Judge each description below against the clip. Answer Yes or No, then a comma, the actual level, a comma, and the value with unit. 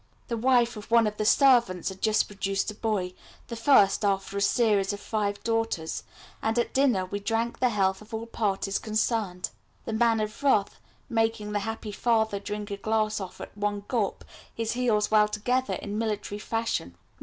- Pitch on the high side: Yes, high, 215 Hz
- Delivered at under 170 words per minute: No, average, 185 wpm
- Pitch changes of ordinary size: No, narrow, 2.0 semitones